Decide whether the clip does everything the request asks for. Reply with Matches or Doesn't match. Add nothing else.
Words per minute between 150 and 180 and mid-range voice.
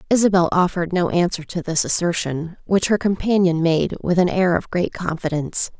Matches